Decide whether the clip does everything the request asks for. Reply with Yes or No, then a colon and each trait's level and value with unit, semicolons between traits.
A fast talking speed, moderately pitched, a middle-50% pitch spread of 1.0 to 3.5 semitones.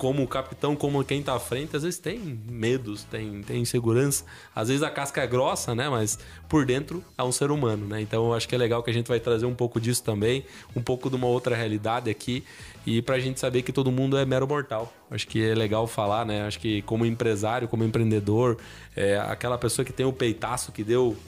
No: fast, 235 wpm; low, 120 Hz; average, 3.0 semitones